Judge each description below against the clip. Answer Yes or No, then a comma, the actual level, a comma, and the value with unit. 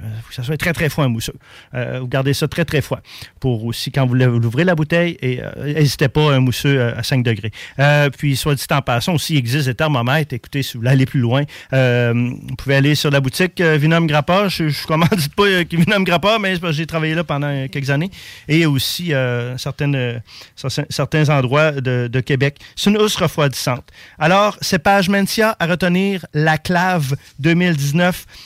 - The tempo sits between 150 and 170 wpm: No, average, 205 wpm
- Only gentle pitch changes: No, average, 4.4 semitones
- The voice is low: No, medium, 145 Hz